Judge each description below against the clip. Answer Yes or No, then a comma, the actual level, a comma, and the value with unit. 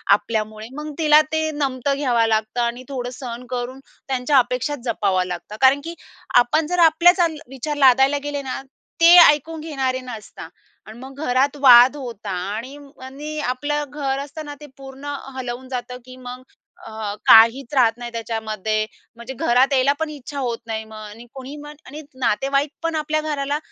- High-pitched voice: Yes, very high, 265 Hz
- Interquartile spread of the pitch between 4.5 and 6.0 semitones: No, average, 3.5 semitones